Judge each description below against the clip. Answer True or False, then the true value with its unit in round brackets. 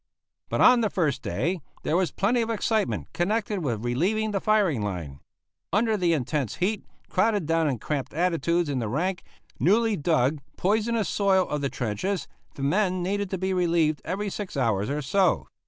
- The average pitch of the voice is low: False (180 Hz)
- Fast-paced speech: False (175 wpm)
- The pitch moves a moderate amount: False (5.9 semitones)